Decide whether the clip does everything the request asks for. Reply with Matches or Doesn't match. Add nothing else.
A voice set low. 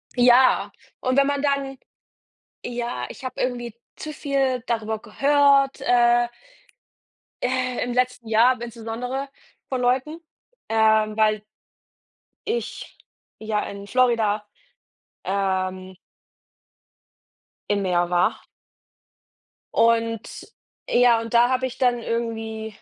Doesn't match